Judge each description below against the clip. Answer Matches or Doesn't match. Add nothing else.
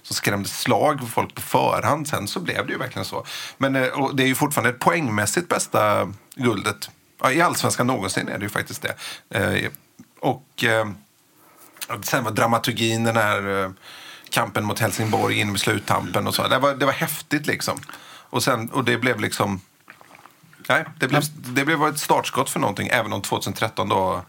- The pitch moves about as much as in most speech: Matches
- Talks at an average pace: Matches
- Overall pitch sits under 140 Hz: Matches